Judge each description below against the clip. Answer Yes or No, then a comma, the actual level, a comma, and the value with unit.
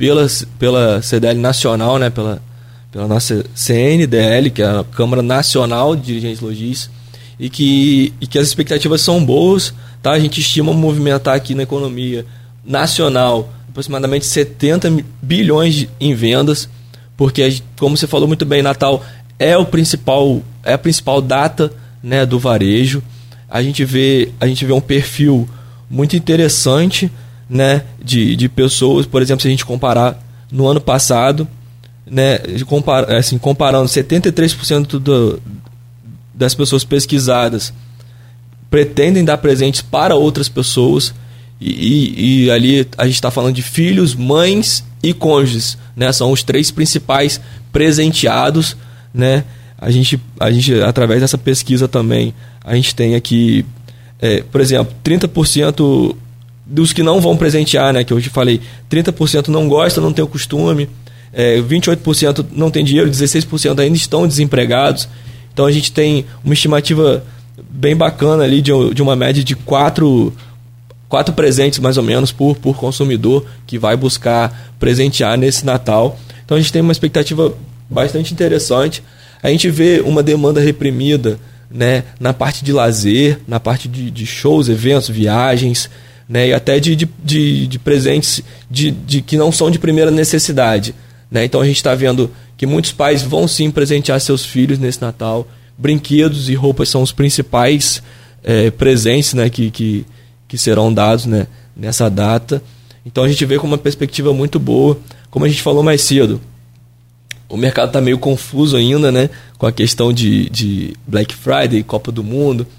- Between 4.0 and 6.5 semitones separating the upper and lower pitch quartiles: No, average, 3.3 semitones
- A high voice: No, low, 130 Hz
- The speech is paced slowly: No, average, 155 wpm